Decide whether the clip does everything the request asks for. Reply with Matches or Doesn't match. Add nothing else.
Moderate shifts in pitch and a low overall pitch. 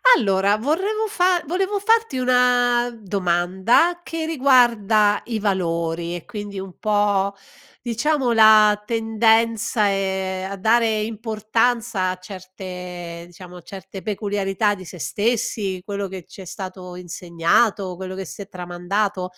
Doesn't match